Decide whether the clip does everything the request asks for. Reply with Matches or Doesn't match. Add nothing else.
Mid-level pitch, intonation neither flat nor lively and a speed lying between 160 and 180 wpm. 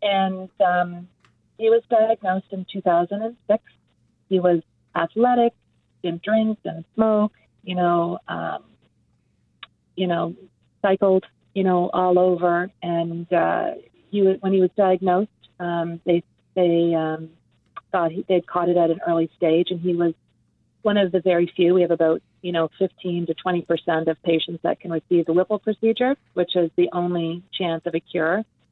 Doesn't match